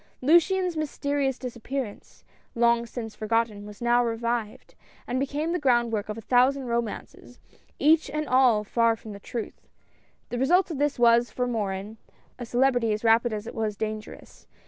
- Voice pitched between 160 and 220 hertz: No, high, 240 Hz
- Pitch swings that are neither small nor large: Yes, average, 3.3 semitones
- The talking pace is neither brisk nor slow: Yes, average, 165 wpm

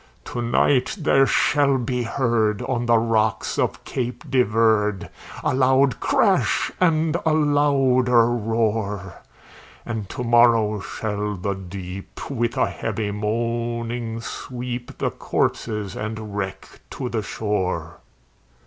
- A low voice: Yes, low, 115 Hz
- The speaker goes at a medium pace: No, slow, 120 wpm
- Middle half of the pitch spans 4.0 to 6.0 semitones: No, average, 3.1 semitones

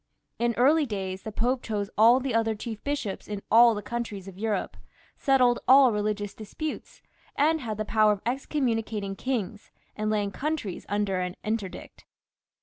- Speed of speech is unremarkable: Yes, average, 160 wpm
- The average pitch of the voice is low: No, high, 220 Hz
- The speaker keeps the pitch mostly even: No, average, 3.3 semitones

